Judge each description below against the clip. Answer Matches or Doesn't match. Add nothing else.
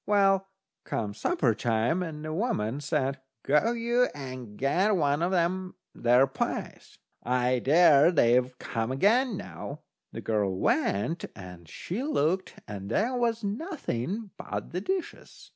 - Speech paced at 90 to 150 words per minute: Matches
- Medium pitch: Matches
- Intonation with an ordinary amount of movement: Doesn't match